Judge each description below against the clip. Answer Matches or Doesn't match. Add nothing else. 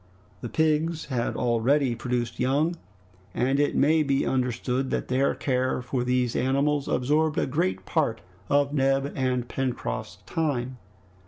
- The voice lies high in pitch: Doesn't match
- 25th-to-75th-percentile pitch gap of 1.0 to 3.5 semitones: Matches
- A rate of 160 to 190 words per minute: Doesn't match